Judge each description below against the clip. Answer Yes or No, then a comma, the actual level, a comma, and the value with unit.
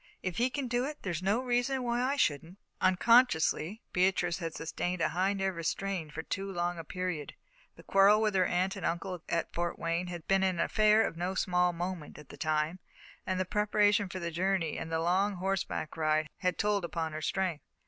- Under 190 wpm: No, fast, 205 wpm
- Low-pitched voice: No, medium, 185 Hz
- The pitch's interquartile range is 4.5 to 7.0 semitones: No, average, 3.1 semitones